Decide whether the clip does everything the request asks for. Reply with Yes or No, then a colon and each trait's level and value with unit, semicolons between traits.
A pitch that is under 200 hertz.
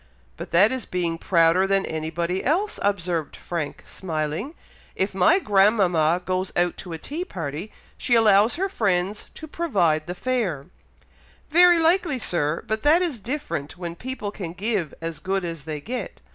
Yes: high, 190 Hz